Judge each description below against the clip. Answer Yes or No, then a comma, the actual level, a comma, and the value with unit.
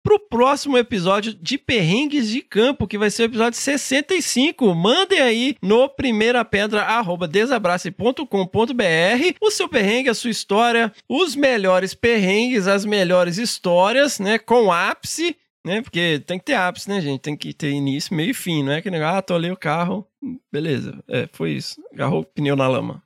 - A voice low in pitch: No, high, 215 Hz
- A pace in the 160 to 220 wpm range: Yes, average, 170 wpm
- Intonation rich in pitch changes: Yes, wide, 5.7 semitones